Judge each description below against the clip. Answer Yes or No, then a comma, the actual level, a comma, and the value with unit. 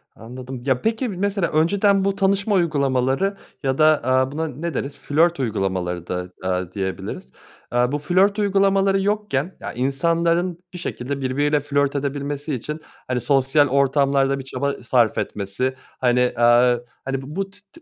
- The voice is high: No, medium, 140 Hz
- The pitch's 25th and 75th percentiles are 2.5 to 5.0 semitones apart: No, wide, 5.6 semitones